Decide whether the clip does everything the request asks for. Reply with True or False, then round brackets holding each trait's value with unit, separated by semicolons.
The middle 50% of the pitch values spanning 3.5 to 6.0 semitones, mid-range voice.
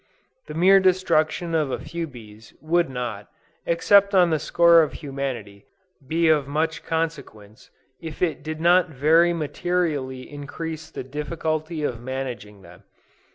True (4.2 semitones; 155 Hz)